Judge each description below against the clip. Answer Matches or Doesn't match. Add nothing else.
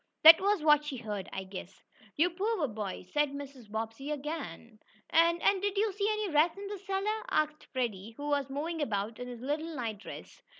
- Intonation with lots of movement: Matches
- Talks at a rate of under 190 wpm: Doesn't match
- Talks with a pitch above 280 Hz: Matches